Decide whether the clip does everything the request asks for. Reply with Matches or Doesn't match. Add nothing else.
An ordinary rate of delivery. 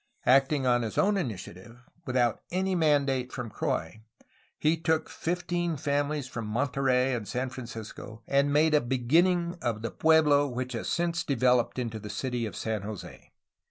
Matches